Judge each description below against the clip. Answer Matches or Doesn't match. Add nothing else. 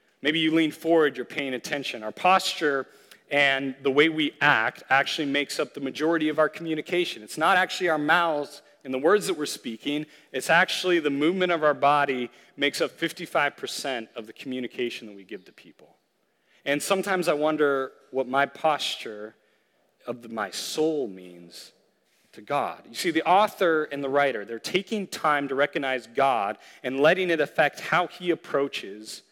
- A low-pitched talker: Doesn't match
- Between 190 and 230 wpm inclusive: Doesn't match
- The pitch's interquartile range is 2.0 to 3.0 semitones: Doesn't match